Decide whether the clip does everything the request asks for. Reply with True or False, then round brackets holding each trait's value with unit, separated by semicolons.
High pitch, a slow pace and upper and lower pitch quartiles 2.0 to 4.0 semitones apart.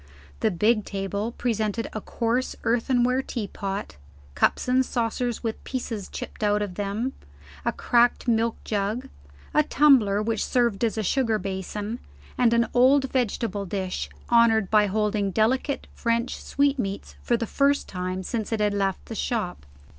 False (225 Hz; 155 wpm; 3.2 semitones)